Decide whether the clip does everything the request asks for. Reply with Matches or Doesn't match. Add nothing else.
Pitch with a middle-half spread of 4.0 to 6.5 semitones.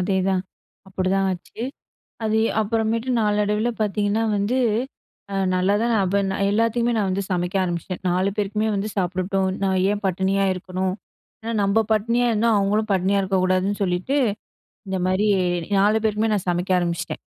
Doesn't match